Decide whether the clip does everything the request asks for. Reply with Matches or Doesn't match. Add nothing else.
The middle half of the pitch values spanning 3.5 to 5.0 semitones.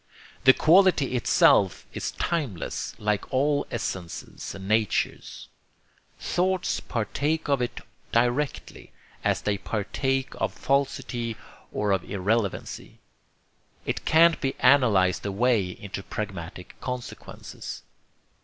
Doesn't match